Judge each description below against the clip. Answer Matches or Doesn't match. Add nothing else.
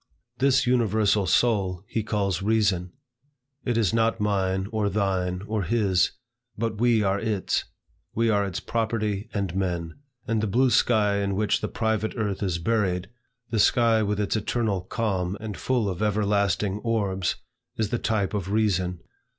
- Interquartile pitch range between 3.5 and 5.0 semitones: Doesn't match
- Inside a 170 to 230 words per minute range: Doesn't match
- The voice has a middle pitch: Doesn't match